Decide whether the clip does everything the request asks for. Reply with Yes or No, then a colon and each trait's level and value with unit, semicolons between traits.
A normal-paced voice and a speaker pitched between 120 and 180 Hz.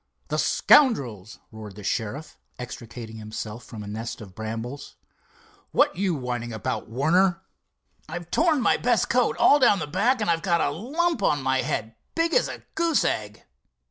Yes: average, 170 wpm; medium, 140 Hz